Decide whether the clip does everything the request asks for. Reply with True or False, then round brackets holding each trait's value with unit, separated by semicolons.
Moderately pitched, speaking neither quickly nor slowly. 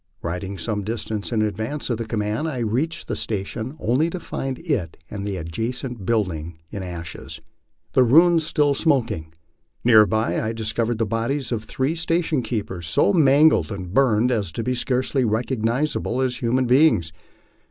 False (115 Hz; 165 wpm)